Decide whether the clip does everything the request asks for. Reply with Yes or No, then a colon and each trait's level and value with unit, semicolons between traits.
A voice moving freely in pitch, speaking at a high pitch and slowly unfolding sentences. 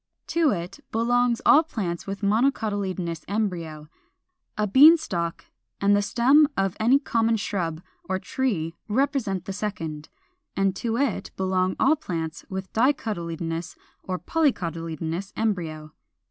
Yes: wide, 5.7 semitones; high, 195 Hz; slow, 130 wpm